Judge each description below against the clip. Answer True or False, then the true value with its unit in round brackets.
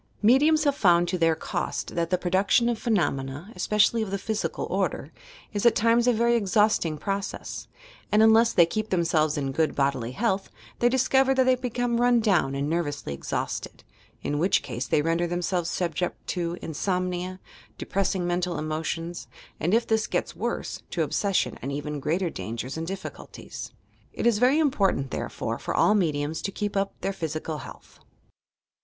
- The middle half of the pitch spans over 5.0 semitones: True (5.5 semitones)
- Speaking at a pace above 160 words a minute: True (170 wpm)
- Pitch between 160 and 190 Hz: True (185 Hz)